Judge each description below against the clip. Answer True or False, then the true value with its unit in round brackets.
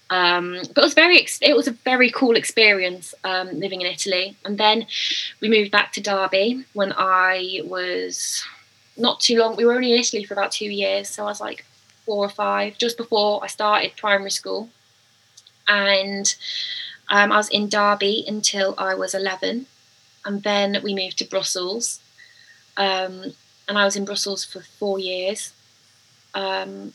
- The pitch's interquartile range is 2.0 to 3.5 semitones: True (2.4 semitones)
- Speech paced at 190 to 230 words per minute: False (170 wpm)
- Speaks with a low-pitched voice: False (200 Hz)